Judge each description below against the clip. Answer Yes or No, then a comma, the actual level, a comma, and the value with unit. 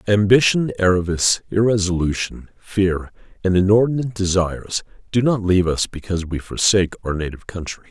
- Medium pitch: No, very low, 95 Hz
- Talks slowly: Yes, slow, 130 wpm